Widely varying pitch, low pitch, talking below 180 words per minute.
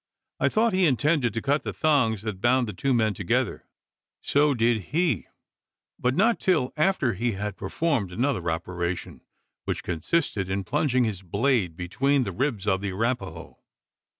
Yes: wide, 6.8 semitones; low, 120 Hz; average, 160 wpm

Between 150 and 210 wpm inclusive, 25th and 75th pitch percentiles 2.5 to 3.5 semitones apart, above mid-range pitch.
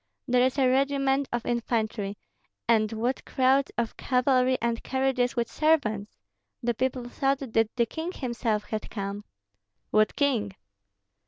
No: average, 140 wpm; average, 3.1 semitones; high, 245 Hz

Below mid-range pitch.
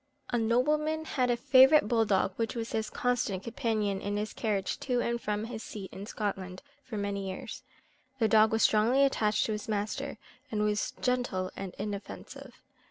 No: high, 220 Hz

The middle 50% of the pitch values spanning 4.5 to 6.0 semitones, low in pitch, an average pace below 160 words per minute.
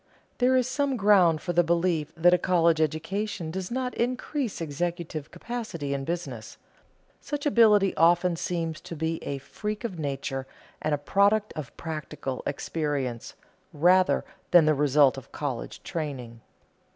No: average, 5.2 semitones; medium, 170 Hz; average, 145 wpm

